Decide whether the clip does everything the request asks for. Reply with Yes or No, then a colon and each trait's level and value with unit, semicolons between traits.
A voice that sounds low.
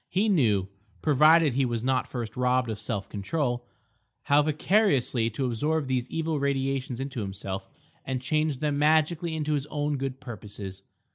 Yes: low, 130 Hz